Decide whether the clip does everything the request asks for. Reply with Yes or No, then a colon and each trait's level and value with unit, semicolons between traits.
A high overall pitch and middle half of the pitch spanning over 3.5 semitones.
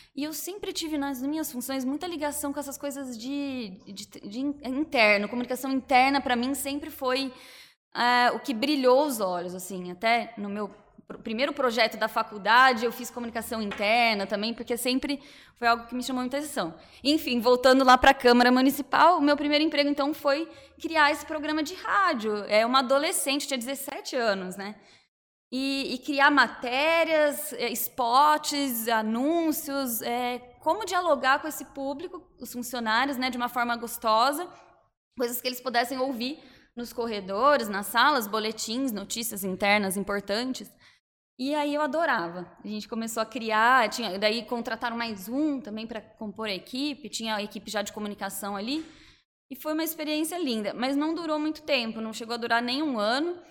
Yes: very high, 255 Hz; average, 4.2 semitones